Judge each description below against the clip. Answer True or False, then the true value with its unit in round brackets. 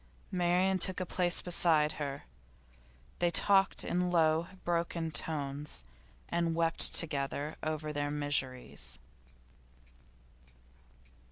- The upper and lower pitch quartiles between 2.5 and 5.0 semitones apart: True (3.0 semitones)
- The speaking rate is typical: False (95 wpm)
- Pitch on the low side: False (165 Hz)